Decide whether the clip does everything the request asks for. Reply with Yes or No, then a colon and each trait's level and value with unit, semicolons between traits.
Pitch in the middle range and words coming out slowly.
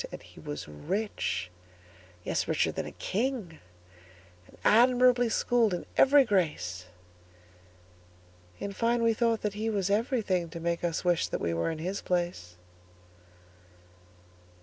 Yes: medium, 165 Hz; slow, 120 wpm